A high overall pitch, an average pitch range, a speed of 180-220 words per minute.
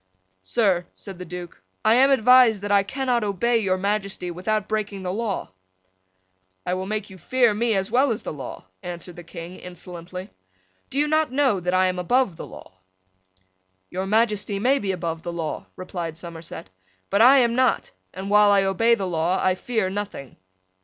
Yes: high, 195 Hz; average, 4.2 semitones; average, 185 wpm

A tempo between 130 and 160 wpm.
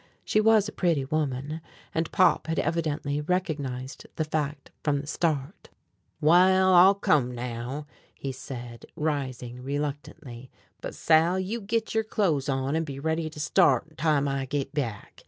Yes: average, 155 wpm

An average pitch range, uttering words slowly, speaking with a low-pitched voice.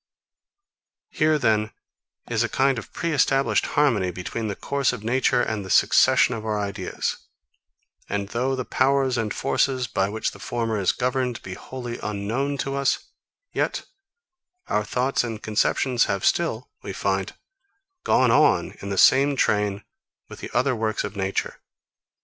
No: average, 4.0 semitones; average, 155 wpm; low, 115 Hz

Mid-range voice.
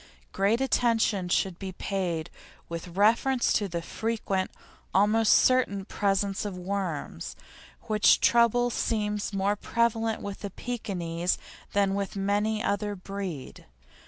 No: high, 200 Hz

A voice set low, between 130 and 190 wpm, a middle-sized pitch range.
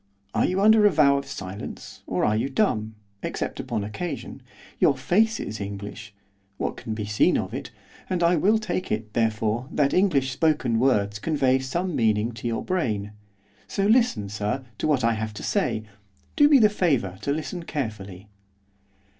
No: low, 130 Hz; average, 175 wpm; wide, 8.4 semitones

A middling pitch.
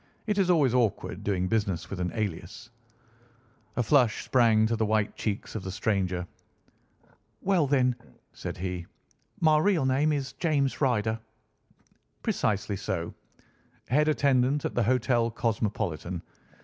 No: low, 115 Hz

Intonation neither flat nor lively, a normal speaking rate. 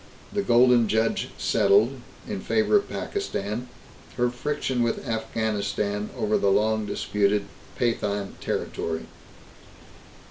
No: average, 3.1 semitones; slow, 105 wpm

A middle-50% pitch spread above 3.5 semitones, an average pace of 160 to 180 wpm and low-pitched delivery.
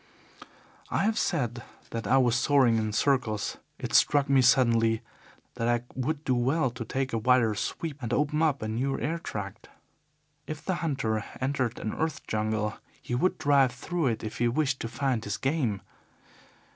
Yes: average, 3.9 semitones; average, 170 wpm; low, 125 Hz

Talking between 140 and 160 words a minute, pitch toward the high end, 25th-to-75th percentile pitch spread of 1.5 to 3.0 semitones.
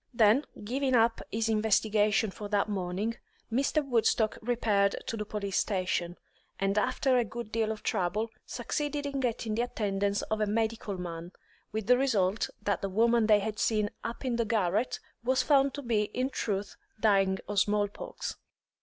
No: average, 170 wpm; high, 220 Hz; average, 2.7 semitones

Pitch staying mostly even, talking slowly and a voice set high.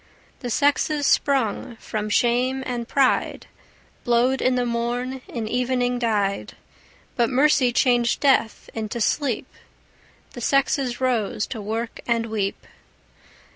Yes: narrow, 2.3 semitones; slow, 120 wpm; high, 245 Hz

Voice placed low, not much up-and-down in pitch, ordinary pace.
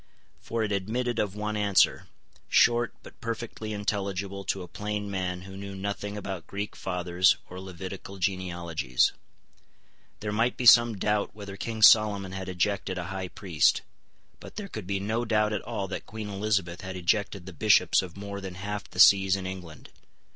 Yes: low, 100 Hz; narrow, 2.2 semitones; average, 175 wpm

